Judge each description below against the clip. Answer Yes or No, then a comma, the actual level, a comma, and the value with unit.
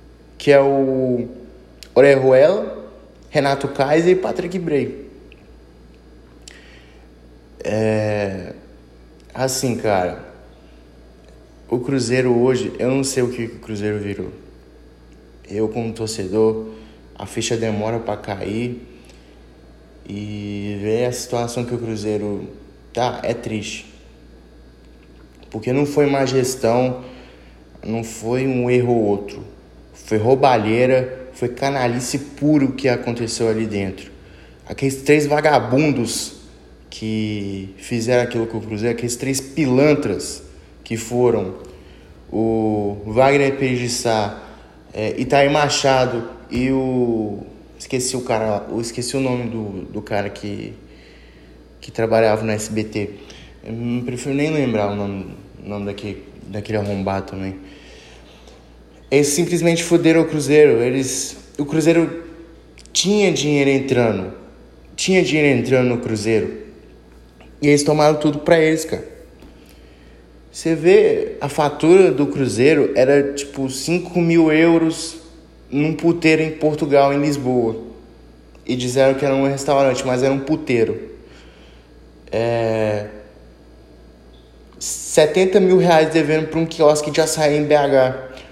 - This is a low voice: Yes, low, 115 Hz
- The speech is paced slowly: Yes, slow, 115 wpm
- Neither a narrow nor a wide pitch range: No, wide, 6.1 semitones